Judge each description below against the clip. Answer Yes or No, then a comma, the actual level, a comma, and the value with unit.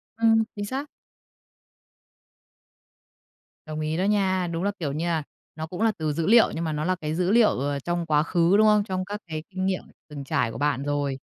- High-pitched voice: No, medium, 170 Hz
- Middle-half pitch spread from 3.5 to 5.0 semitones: Yes, average, 4.7 semitones